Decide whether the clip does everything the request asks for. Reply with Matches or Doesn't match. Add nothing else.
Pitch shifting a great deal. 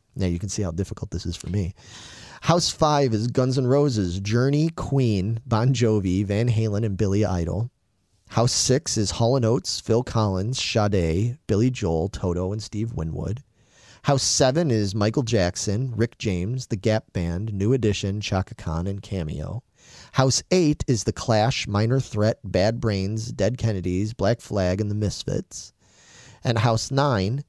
Doesn't match